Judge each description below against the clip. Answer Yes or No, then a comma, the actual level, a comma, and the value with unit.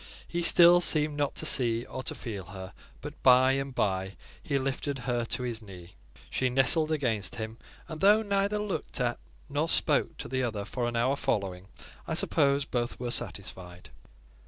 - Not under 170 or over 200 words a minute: Yes, average, 180 wpm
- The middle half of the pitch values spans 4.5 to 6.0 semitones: Yes, average, 4.8 semitones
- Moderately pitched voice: No, low, 125 Hz